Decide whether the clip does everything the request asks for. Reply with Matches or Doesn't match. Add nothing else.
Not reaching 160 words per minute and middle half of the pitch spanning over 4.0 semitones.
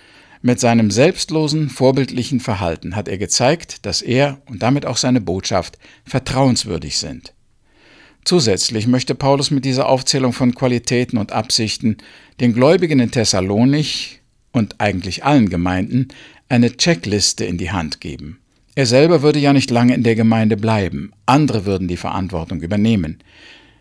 Matches